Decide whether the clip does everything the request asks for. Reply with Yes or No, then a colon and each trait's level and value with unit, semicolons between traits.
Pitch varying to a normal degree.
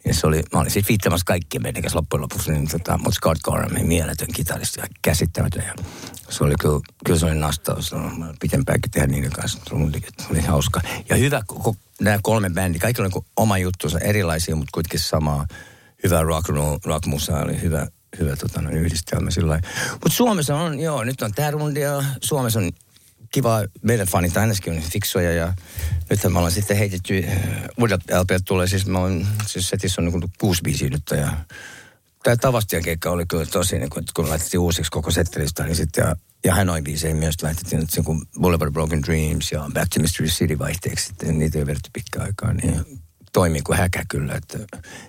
Yes: average, 4.6 semitones